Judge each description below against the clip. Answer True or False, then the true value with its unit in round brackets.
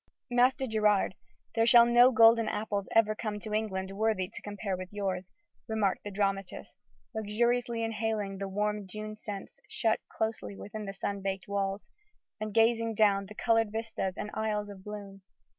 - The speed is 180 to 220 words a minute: False (160 wpm)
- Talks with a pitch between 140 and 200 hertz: False (210 Hz)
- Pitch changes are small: True (2.1 semitones)